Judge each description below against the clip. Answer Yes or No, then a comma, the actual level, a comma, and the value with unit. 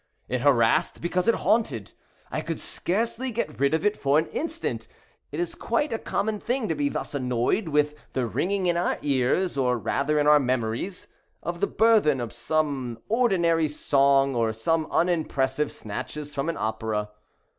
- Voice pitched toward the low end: No, medium, 150 Hz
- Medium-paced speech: Yes, average, 170 wpm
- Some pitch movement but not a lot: No, wide, 6.0 semitones